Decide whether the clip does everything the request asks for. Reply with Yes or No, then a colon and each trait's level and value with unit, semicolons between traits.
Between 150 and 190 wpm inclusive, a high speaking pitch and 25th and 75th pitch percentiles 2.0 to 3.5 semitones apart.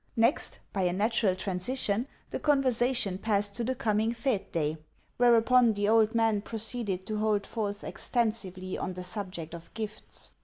Yes: average, 155 wpm; high, 215 Hz; average, 3.2 semitones